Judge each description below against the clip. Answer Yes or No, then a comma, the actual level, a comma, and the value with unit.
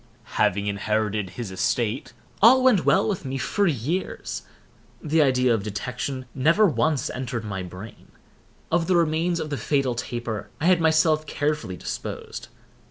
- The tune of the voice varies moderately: No, wide, 6.9 semitones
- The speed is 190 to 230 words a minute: No, average, 150 wpm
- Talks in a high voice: No, low, 135 Hz